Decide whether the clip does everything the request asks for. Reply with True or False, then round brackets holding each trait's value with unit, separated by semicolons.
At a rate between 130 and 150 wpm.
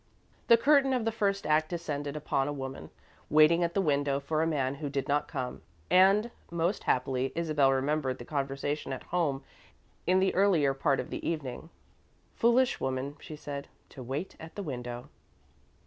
False (175 wpm)